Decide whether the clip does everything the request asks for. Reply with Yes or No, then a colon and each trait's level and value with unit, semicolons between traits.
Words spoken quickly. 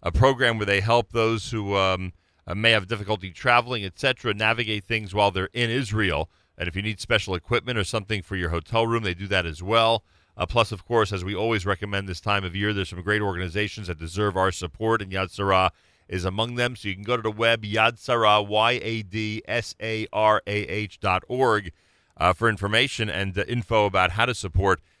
Yes: fast, 220 wpm